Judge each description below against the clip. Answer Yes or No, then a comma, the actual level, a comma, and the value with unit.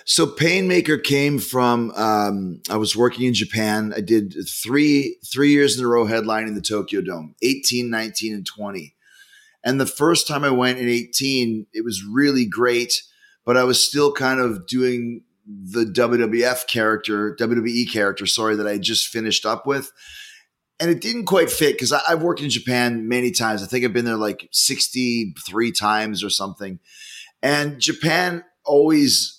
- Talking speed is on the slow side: No, average, 165 wpm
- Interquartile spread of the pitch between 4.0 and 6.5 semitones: Yes, average, 4.5 semitones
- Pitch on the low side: Yes, low, 120 Hz